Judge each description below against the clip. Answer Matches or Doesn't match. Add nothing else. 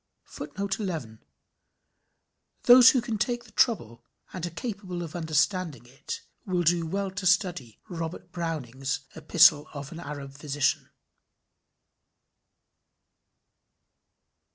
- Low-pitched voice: Doesn't match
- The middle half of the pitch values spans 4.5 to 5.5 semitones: Matches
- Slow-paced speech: Matches